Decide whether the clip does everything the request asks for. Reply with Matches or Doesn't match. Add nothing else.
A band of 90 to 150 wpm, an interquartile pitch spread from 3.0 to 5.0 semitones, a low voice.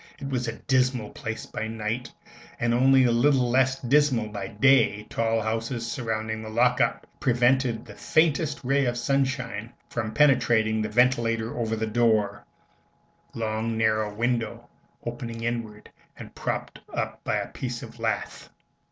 Doesn't match